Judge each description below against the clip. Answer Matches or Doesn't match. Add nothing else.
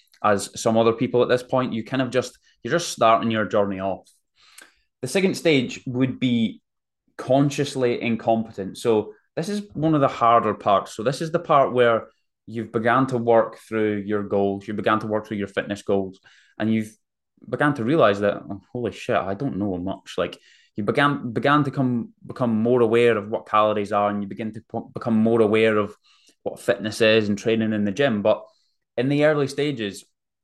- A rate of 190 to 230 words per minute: Matches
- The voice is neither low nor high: Doesn't match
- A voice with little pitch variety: Doesn't match